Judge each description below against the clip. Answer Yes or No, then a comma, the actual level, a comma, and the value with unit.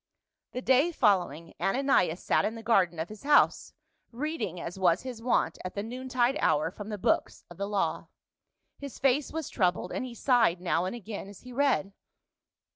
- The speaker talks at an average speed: Yes, average, 185 wpm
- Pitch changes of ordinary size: No, wide, 5.9 semitones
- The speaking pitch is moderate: No, high, 220 Hz